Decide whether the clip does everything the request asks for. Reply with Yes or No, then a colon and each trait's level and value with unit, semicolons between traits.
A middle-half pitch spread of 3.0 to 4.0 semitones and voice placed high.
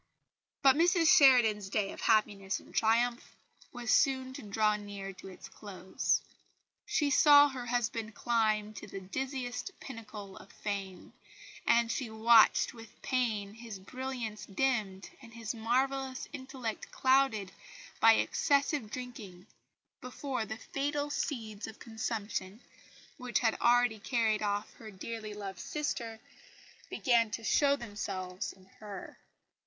Yes: average, 3.7 semitones; high, 225 Hz